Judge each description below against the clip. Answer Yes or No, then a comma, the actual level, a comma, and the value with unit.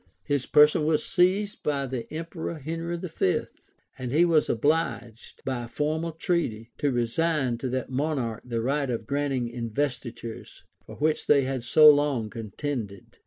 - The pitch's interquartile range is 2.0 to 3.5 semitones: No, average, 4.7 semitones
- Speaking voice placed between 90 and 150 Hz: Yes, medium, 140 Hz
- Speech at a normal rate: Yes, average, 155 wpm